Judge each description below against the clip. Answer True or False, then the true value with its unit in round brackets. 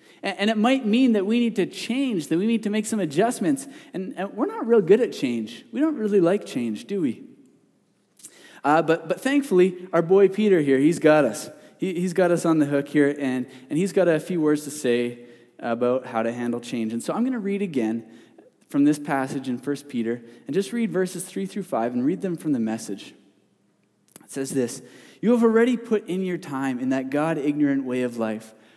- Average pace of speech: False (220 wpm)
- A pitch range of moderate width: False (8.0 semitones)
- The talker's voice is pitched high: False (160 Hz)